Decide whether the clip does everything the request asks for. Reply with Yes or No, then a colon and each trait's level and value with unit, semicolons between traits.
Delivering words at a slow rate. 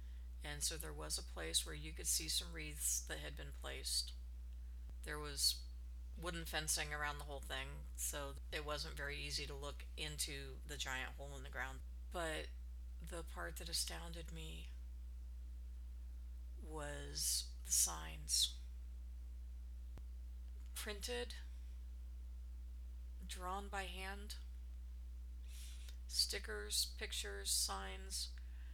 Yes: slow, 115 wpm